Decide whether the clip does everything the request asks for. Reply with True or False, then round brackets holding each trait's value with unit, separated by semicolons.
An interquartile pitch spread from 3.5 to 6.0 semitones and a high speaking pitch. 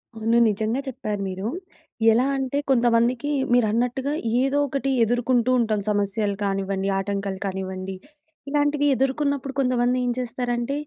True (4.3 semitones; 240 Hz)